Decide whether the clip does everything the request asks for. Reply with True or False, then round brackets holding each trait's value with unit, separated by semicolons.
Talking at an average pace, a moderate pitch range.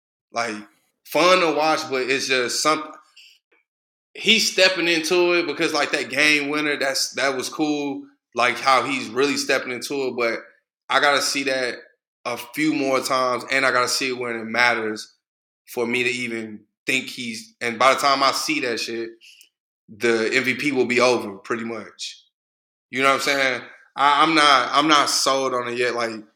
True (185 wpm; 3.9 semitones)